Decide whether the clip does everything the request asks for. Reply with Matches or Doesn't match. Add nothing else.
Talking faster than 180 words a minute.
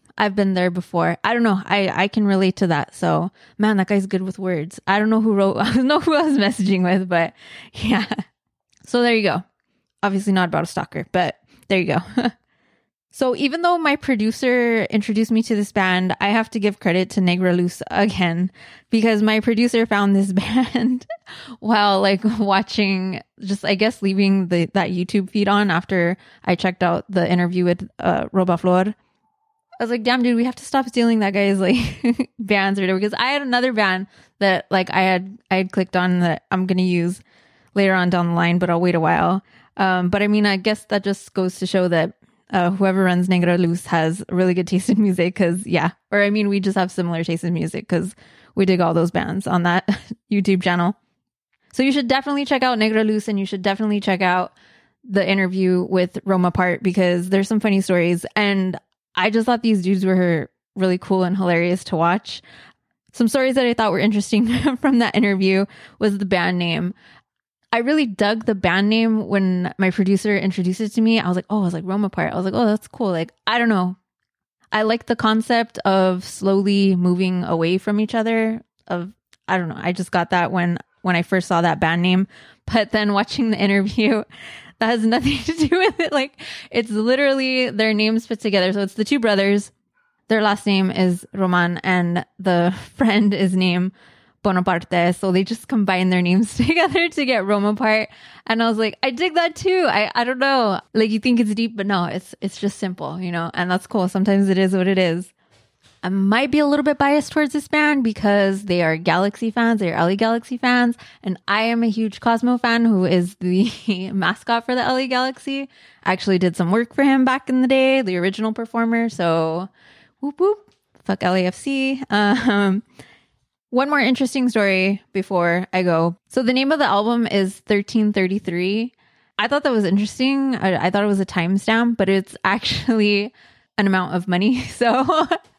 Matches